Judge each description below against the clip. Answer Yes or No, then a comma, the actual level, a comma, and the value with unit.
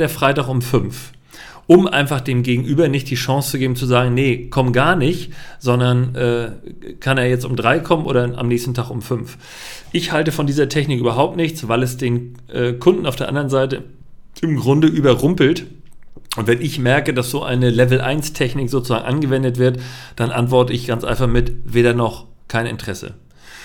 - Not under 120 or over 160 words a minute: No, fast, 190 wpm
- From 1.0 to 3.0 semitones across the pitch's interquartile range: Yes, narrow, 2.6 semitones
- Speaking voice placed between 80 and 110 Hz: No, low, 130 Hz